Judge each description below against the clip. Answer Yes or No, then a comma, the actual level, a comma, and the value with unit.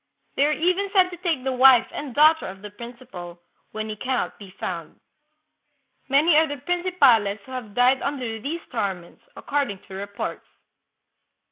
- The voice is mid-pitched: No, very high, 255 Hz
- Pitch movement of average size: No, wide, 6.6 semitones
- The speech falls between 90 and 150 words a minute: No, average, 170 wpm